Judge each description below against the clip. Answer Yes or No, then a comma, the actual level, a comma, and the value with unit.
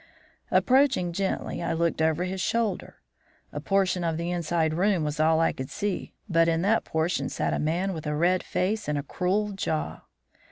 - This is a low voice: No, medium, 175 Hz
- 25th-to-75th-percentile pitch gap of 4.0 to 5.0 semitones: No, average, 3.3 semitones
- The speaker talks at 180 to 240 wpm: Yes, average, 190 wpm